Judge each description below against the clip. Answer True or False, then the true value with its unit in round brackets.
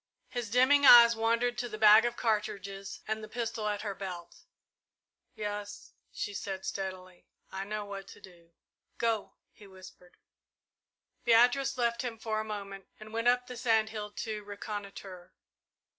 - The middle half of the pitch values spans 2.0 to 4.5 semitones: True (2.8 semitones)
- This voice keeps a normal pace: True (155 wpm)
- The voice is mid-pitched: False (215 Hz)